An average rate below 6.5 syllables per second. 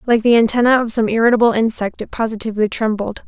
No: 6.8 syllables/s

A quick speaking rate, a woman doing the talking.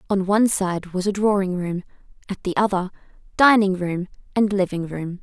No: average, 170 wpm; female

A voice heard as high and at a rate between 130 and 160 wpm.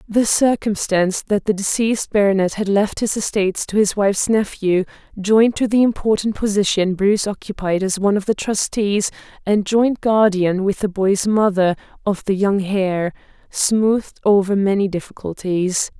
Yes: high, 200 Hz; average, 155 wpm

